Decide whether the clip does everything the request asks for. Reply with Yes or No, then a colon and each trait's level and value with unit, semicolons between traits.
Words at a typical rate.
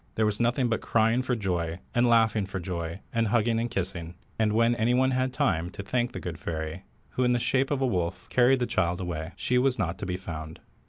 No: fast, 235 wpm